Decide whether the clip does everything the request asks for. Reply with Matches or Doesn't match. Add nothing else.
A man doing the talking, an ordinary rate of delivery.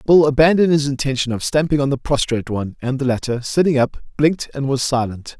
Doesn't match